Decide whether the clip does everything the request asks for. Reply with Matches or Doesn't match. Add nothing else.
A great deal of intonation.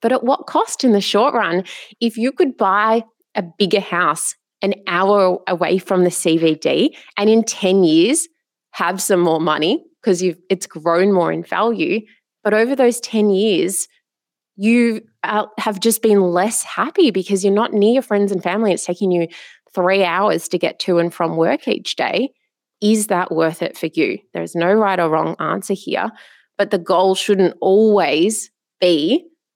Doesn't match